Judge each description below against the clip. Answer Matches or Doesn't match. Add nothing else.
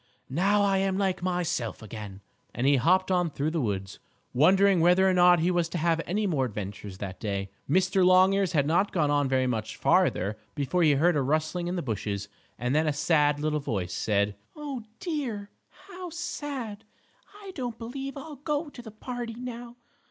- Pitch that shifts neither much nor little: Doesn't match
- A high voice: Doesn't match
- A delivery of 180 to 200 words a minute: Matches